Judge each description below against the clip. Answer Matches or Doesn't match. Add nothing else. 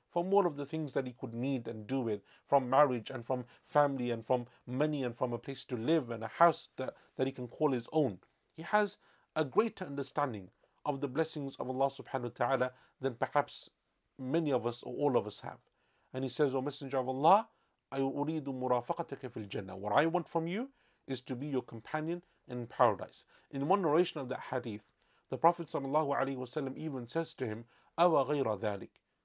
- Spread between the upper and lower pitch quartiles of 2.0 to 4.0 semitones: Matches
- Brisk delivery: Doesn't match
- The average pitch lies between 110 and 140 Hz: Matches